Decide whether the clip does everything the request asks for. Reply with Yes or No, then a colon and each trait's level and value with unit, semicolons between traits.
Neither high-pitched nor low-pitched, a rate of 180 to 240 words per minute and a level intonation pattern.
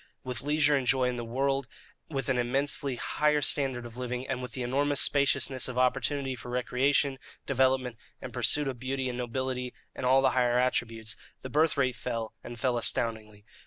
No: low, 130 Hz; average, 185 wpm; narrow, 1.9 semitones